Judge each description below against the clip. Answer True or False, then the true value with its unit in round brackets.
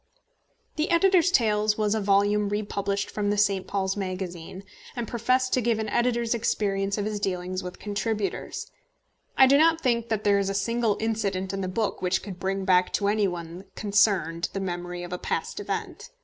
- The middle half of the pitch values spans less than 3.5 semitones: True (2.8 semitones)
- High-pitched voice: True (205 Hz)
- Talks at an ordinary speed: True (190 wpm)